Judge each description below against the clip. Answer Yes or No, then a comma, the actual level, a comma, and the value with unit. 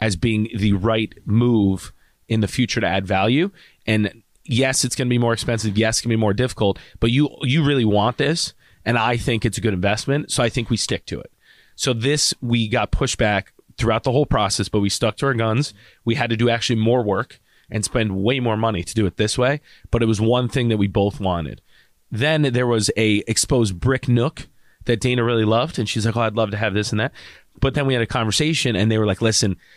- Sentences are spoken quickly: Yes, fast, 245 wpm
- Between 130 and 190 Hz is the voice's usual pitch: No, low, 115 Hz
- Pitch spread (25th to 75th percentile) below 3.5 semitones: Yes, average, 2.8 semitones